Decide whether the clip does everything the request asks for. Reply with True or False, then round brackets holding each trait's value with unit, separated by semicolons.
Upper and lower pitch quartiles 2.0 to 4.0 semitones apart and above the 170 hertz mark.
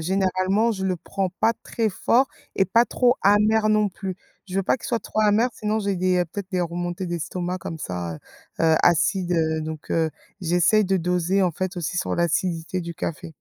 True (3.0 semitones; 185 Hz)